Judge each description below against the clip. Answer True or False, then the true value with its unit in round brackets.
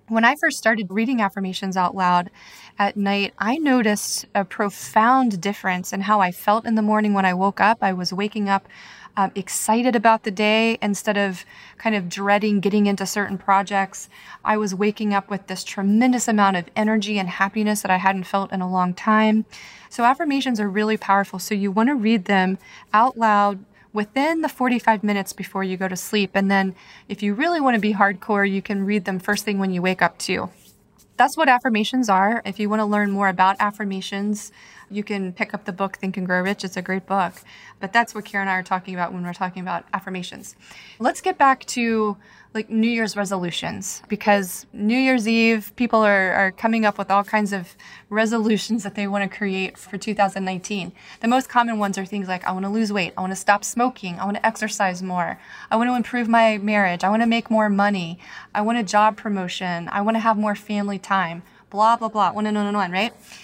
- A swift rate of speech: True (220 wpm)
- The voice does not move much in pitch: True (2.2 semitones)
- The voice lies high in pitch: True (205 Hz)